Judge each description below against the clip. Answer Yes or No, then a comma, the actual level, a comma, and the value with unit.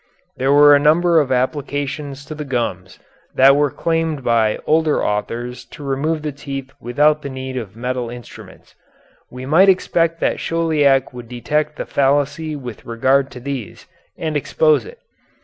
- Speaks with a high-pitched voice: No, medium, 140 Hz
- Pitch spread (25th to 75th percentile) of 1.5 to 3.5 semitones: Yes, average, 3.2 semitones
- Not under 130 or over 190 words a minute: Yes, average, 160 wpm